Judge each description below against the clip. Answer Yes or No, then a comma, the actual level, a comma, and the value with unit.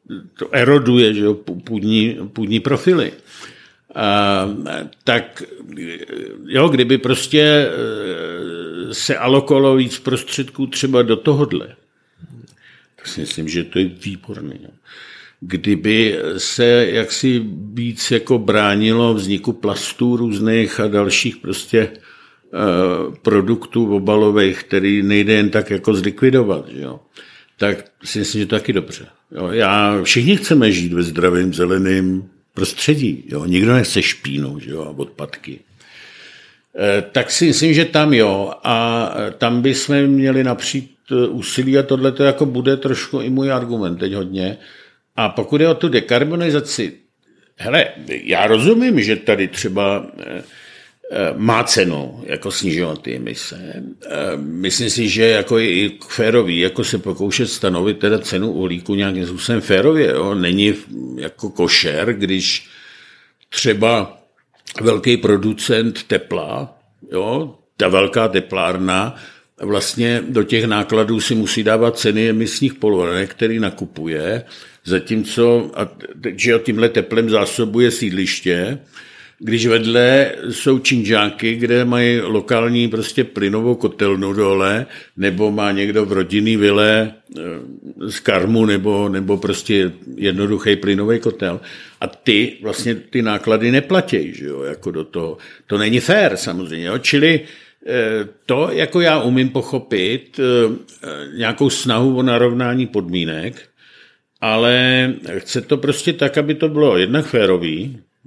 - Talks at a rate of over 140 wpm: No, average, 125 wpm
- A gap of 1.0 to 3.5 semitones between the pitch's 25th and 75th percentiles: No, average, 4.2 semitones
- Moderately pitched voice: No, low, 115 Hz